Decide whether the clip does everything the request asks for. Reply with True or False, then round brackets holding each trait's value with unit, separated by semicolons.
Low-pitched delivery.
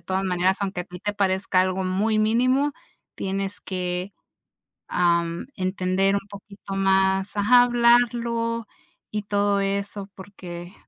False (195 Hz)